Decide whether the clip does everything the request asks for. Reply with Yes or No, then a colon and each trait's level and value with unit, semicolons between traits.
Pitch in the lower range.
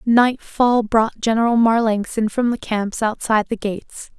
No: high, 225 Hz